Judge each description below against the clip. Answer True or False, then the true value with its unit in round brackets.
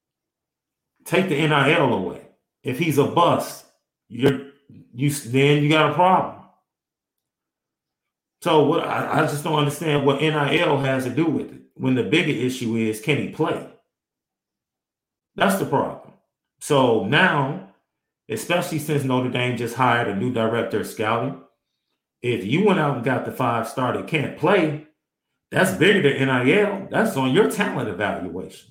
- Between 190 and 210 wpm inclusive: False (155 wpm)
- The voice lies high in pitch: False (140 Hz)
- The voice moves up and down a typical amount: True (3.4 semitones)